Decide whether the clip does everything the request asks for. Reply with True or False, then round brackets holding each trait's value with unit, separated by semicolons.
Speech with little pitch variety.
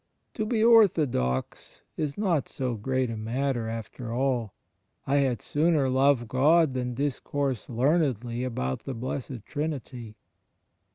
False (3.7 semitones)